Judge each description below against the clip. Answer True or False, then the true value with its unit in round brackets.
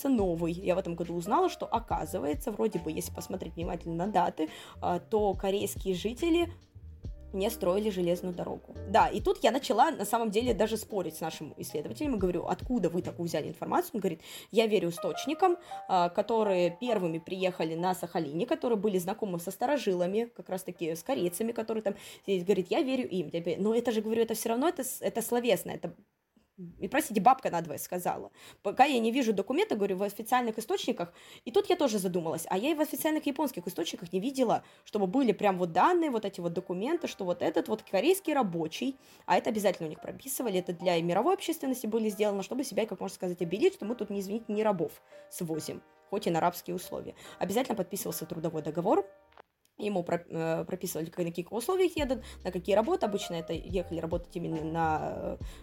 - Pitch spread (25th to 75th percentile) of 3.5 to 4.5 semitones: False (5.3 semitones)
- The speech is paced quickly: True (190 wpm)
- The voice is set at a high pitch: True (195 Hz)